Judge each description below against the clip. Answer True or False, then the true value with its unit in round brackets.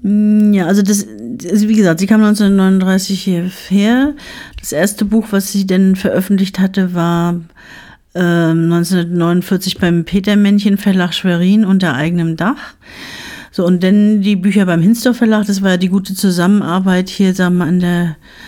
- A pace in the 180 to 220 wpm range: False (150 wpm)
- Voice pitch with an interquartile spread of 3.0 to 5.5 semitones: False (2.5 semitones)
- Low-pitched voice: False (190 Hz)